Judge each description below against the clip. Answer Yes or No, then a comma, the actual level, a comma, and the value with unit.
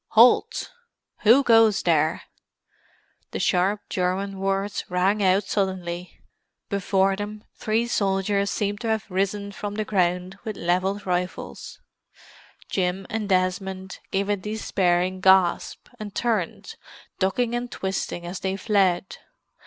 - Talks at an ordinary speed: No, slow, 120 wpm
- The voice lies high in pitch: Yes, high, 195 Hz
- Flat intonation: Yes, narrow, 2.2 semitones